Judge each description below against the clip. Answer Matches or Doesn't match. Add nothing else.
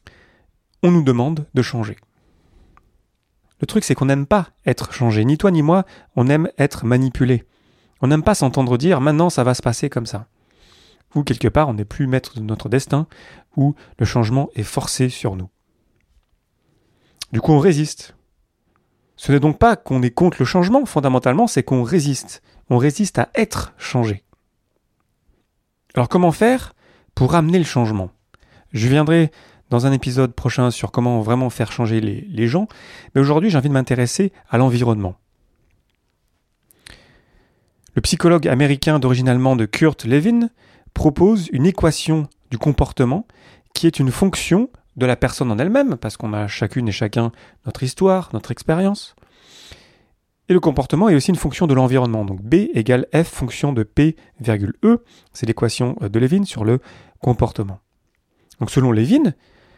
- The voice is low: Matches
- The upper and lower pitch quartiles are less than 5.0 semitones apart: Doesn't match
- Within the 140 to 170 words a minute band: Matches